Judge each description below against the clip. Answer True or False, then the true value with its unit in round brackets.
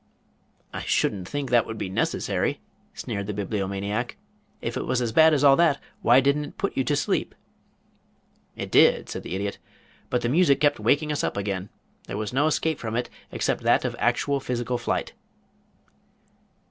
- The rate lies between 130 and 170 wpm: False (180 wpm)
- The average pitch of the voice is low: True (125 Hz)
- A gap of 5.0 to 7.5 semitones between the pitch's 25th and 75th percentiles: True (5.5 semitones)